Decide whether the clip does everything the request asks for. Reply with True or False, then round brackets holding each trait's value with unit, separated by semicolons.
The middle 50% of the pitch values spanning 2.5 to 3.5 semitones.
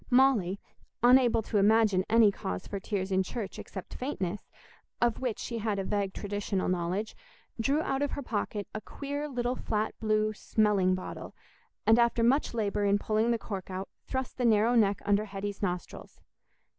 True (3.2 semitones)